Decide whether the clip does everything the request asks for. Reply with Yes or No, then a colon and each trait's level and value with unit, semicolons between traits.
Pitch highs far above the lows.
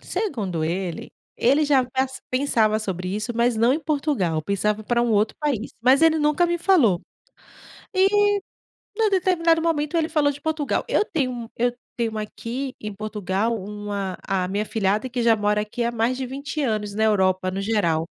Yes: wide, 5.7 semitones